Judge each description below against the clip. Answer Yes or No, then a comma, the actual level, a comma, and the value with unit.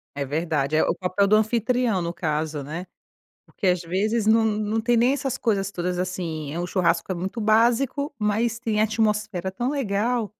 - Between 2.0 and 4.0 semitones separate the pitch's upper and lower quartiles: No, average, 4.4 semitones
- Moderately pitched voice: No, high, 205 Hz